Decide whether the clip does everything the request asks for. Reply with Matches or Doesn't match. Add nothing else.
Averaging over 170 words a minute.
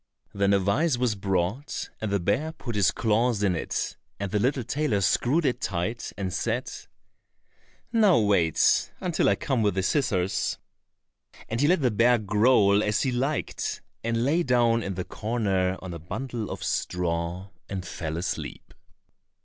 Doesn't match